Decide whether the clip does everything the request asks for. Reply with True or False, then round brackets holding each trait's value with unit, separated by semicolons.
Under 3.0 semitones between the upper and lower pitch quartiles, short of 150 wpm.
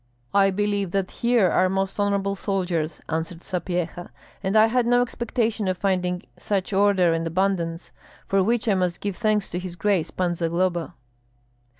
False (2.5 semitones; 165 wpm)